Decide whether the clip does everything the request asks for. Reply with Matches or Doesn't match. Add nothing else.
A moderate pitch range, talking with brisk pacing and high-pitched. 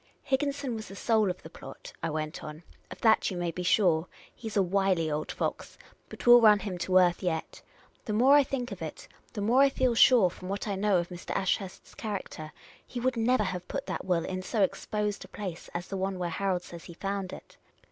Matches